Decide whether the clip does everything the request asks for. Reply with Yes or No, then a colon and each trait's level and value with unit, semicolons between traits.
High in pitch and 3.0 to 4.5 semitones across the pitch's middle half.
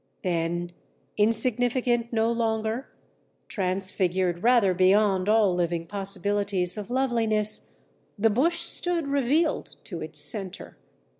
Yes: high, 210 Hz; average, 4.2 semitones